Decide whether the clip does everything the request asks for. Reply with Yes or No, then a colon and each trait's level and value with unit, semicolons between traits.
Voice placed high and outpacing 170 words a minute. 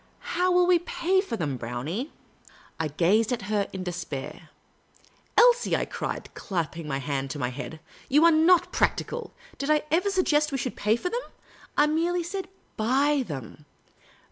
Yes: high, 245 Hz; average, 190 wpm